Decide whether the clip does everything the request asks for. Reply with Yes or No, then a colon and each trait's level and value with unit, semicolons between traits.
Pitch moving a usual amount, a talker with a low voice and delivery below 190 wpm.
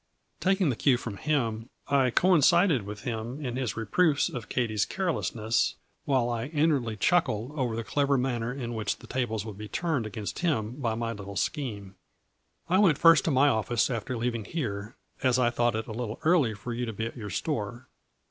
No: average, 4.4 semitones; low, 120 Hz; average, 200 wpm